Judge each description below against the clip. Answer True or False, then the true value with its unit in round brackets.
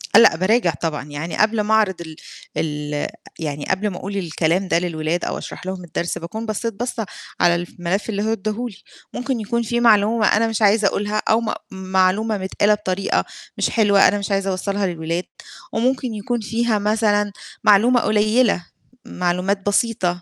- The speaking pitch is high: True (200 Hz)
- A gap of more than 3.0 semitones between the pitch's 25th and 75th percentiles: True (3.6 semitones)